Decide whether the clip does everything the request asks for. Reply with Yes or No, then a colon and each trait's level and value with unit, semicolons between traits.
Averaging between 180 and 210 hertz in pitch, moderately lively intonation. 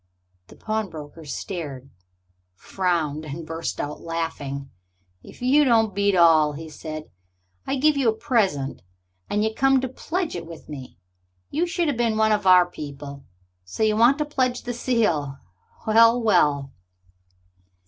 No: medium, 185 Hz; wide, 7.8 semitones